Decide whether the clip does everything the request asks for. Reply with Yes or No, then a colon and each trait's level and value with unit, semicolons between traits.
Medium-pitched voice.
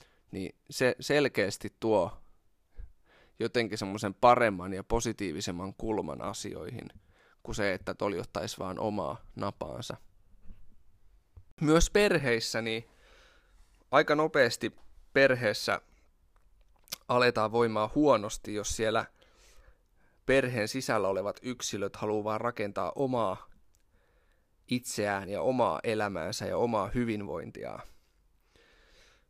No: low, 105 Hz